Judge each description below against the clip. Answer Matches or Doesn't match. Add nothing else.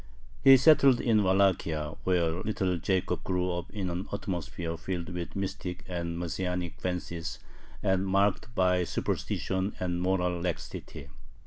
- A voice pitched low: Matches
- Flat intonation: Matches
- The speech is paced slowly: Matches